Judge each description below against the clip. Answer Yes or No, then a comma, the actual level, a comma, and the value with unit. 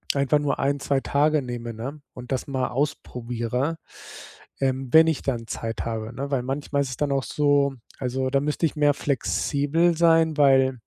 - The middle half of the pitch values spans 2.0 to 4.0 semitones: Yes, narrow, 2.6 semitones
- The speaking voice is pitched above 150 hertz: No, medium, 140 Hz